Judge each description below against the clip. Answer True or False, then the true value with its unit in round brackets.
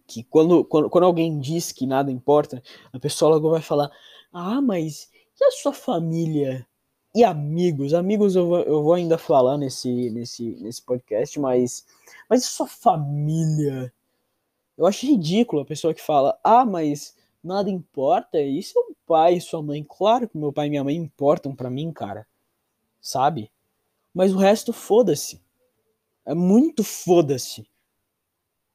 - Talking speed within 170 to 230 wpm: False (155 wpm)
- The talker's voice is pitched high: False (155 Hz)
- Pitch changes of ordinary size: False (5.8 semitones)